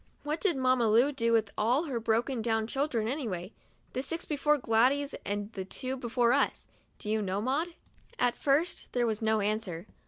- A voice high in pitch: Yes, high, 240 Hz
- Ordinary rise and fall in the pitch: Yes, average, 4.0 semitones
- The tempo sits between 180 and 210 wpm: Yes, average, 190 wpm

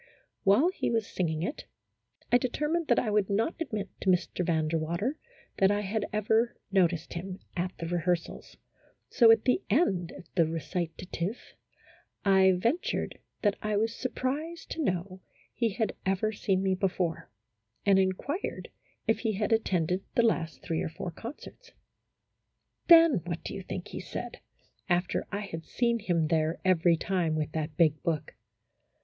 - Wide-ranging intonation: No, average, 4.8 semitones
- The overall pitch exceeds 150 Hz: Yes, high, 190 Hz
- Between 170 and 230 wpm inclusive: No, average, 160 wpm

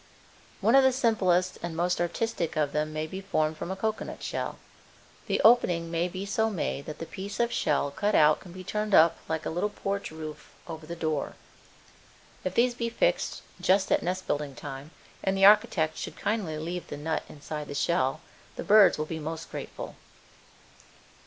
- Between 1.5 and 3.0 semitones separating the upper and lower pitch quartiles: No, average, 4.5 semitones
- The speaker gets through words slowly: No, average, 190 wpm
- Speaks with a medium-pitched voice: Yes, medium, 175 Hz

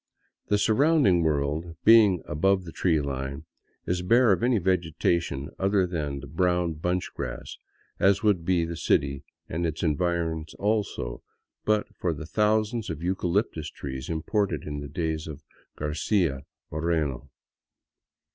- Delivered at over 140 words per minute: No, slow, 135 wpm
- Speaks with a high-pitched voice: No, very low, 85 Hz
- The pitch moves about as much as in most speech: Yes, average, 4.3 semitones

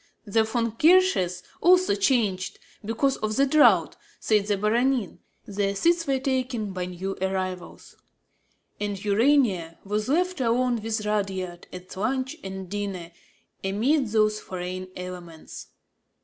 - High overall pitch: Yes, high, 210 Hz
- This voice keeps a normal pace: No, slow, 125 wpm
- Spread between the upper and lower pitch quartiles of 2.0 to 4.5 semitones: No, average, 5.2 semitones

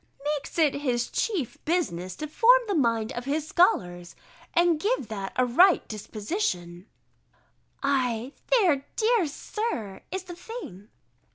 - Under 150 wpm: Yes, average, 140 wpm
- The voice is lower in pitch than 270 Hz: No, very high, 280 Hz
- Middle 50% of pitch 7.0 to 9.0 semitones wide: Yes, wide, 8.5 semitones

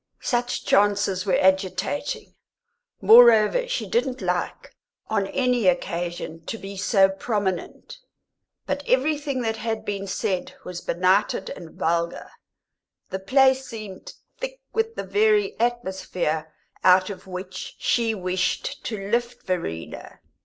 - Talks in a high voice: Yes, high, 205 Hz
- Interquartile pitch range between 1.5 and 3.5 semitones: No, average, 4.9 semitones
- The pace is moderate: No, slow, 120 wpm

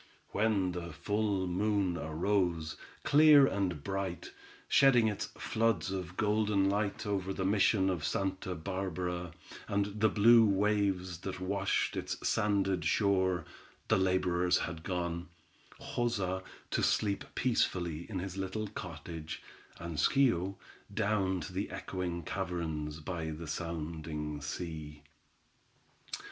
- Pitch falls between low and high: No, very low, 95 Hz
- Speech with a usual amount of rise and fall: Yes, average, 3.0 semitones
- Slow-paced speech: Yes, slow, 115 wpm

